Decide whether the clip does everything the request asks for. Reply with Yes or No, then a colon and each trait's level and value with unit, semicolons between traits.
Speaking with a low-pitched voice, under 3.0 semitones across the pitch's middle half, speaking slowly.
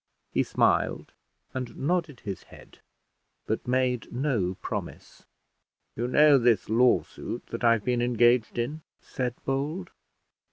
Yes: low, 125 Hz; narrow, 2.5 semitones; slow, 120 wpm